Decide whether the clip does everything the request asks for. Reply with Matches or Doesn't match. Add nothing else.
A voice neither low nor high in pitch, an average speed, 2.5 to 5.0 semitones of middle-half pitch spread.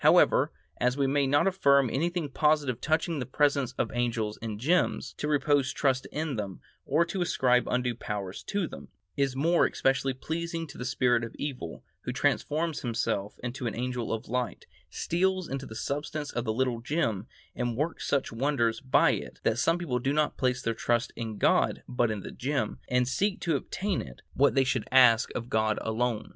Doesn't match